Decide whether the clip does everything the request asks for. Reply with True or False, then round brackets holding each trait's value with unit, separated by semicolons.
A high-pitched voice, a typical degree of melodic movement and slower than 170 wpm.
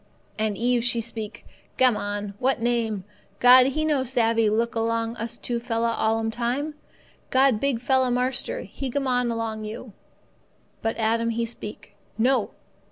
False (235 Hz; 2.0 semitones; 150 wpm)